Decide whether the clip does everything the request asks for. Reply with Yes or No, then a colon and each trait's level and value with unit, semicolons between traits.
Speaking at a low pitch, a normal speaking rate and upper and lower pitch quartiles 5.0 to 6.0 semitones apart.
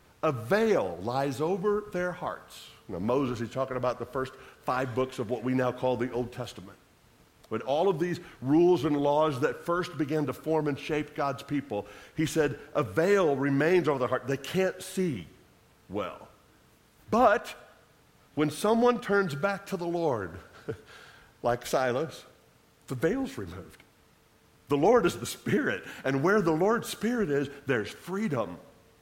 No: medium, 145 Hz; average, 160 wpm; wide, 5.5 semitones